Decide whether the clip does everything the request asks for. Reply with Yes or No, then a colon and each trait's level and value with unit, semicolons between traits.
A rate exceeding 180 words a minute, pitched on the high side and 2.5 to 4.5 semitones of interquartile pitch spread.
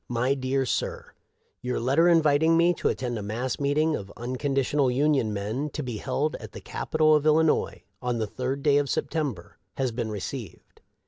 No: average, 195 wpm; low, 135 Hz; average, 3.9 semitones